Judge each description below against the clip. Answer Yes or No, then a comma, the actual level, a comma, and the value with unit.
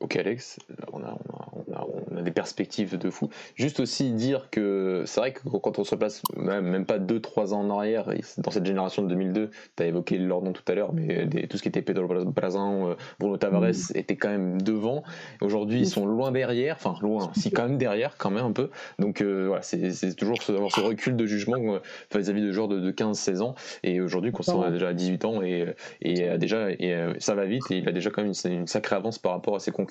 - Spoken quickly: Yes, fast, 255 wpm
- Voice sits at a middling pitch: No, low, 100 Hz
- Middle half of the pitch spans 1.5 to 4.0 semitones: Yes, average, 2.9 semitones